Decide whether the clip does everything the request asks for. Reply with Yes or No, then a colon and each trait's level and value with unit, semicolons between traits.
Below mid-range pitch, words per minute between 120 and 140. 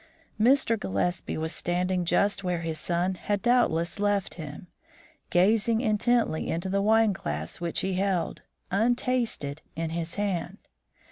No: medium, 185 Hz; slow, 135 wpm